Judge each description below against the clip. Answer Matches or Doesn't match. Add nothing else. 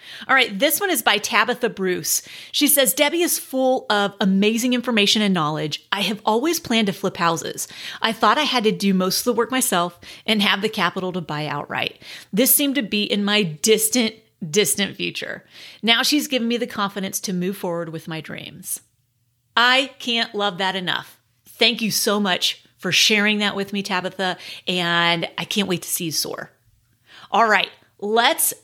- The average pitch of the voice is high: Matches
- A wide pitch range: Doesn't match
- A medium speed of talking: Matches